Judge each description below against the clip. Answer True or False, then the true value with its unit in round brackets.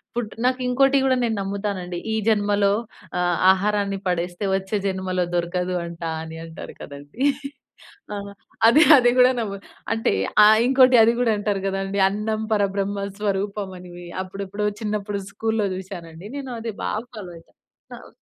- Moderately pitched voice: False (200 Hz)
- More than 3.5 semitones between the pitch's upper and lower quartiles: False (2.8 semitones)